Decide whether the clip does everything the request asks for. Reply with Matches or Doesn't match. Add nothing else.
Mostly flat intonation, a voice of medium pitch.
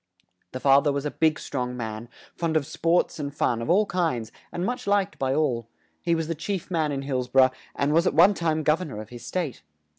Doesn't match